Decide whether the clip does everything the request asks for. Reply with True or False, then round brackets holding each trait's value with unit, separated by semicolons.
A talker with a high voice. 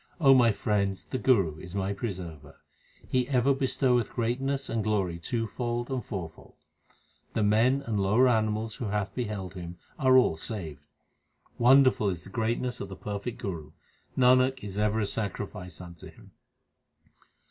False (110 Hz)